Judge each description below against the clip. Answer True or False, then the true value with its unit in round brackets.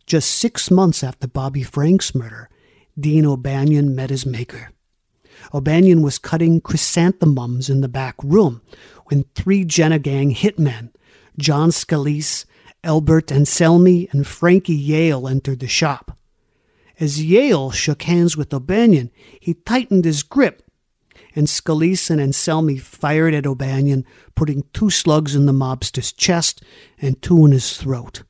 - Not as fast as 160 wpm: True (135 wpm)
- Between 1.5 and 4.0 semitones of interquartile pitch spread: True (3.5 semitones)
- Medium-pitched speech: True (150 Hz)